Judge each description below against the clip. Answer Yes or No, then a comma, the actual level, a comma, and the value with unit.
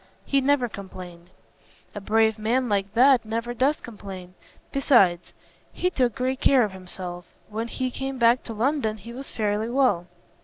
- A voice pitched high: Yes, high, 225 Hz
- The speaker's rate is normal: Yes, average, 160 wpm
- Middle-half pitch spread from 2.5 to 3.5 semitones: No, average, 4.5 semitones